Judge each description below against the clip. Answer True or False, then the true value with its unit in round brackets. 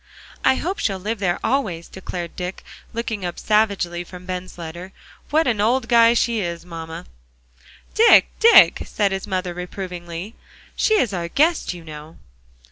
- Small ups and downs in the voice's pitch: False (4.8 semitones)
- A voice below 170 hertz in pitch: False (190 Hz)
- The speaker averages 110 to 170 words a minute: True (155 wpm)